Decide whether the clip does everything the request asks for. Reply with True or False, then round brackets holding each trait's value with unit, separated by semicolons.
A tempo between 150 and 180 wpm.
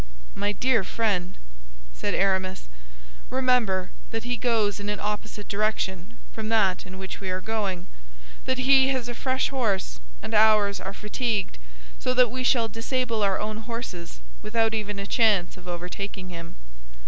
True (160 wpm)